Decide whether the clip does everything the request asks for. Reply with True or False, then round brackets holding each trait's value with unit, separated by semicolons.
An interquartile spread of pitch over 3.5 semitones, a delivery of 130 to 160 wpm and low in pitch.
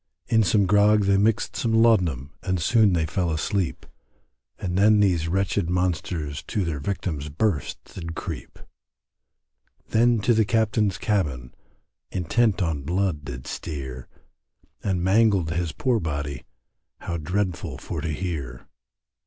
True (4.8 semitones; 135 wpm; 90 Hz)